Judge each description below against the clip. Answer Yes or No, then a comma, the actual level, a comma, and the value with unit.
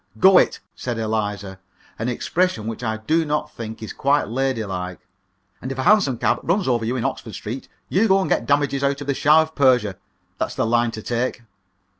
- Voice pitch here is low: Yes, low, 125 Hz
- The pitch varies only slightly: No, average, 4.6 semitones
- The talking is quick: Yes, fast, 215 wpm